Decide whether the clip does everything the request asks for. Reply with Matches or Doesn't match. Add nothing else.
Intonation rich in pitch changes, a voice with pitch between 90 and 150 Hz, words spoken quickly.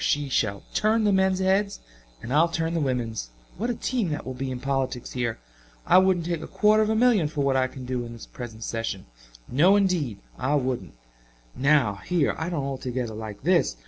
Matches